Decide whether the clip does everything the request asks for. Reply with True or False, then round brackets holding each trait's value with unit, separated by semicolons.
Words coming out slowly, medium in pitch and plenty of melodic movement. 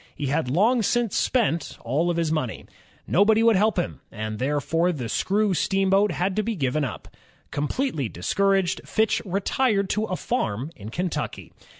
False (165 wpm; 180 Hz; 6.3 semitones)